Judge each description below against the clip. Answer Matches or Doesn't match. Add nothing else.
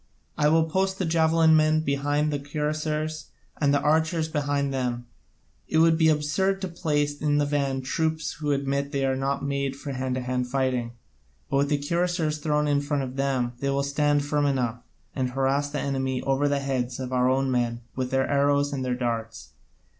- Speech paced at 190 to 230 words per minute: Matches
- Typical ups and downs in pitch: Doesn't match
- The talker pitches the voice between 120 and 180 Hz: Matches